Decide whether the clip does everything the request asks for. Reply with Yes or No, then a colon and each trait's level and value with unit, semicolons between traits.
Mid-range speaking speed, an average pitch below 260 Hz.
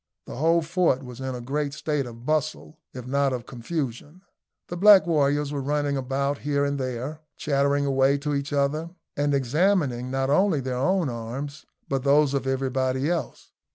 Yes: average, 175 wpm; medium, 140 Hz